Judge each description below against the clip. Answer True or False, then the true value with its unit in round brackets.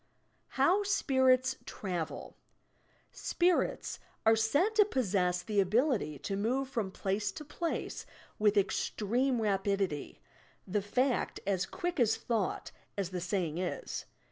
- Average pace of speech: False (125 wpm)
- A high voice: True (215 Hz)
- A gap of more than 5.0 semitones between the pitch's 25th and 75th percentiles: True (5.6 semitones)